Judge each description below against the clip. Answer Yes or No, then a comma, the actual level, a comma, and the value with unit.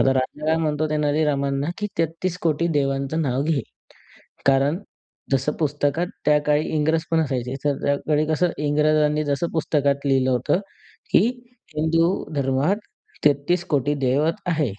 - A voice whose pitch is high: No, medium, 150 Hz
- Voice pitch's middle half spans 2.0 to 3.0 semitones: Yes, narrow, 2.4 semitones